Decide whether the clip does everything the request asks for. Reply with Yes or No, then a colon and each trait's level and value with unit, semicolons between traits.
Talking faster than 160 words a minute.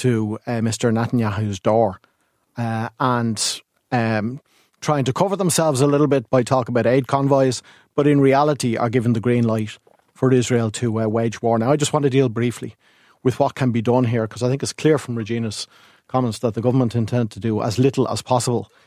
Yes: fast, 205 wpm